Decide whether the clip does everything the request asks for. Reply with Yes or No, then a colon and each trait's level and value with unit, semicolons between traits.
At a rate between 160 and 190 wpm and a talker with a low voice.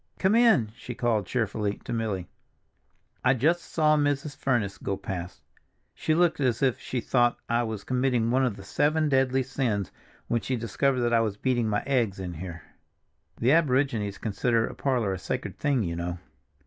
Yes: average, 180 wpm; low, 120 Hz